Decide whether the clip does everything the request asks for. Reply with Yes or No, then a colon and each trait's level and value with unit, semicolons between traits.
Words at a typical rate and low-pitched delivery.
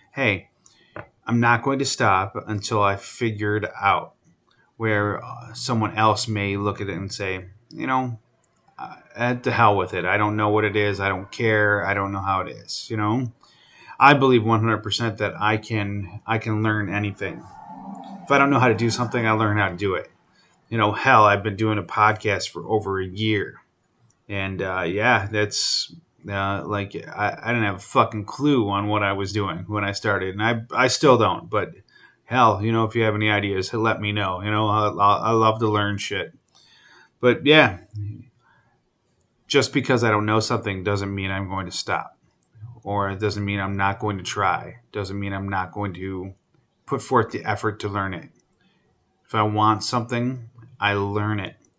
Yes: average, 195 wpm; low, 105 Hz